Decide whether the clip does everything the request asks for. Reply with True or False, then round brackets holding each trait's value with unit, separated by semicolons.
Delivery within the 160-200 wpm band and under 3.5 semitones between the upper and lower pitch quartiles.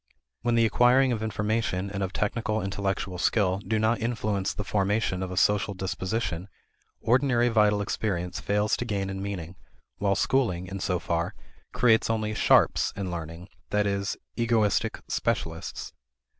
False (150 wpm; 2.8 semitones)